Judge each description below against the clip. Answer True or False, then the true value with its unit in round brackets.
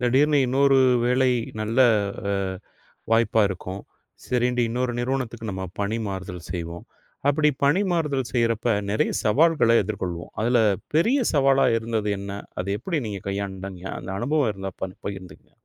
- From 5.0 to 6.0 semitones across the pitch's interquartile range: True (5.4 semitones)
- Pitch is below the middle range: True (115 Hz)